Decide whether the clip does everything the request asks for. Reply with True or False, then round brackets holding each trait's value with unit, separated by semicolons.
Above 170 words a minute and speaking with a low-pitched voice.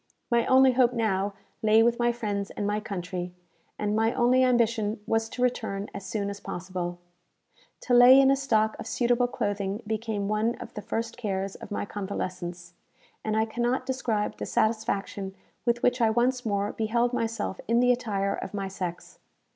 False (180 wpm; 220 Hz)